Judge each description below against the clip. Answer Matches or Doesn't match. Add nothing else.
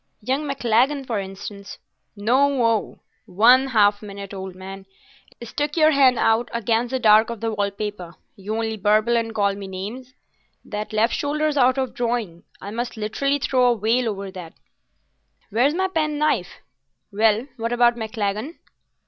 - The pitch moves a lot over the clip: Doesn't match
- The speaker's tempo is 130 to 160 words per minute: Matches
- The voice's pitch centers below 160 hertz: Doesn't match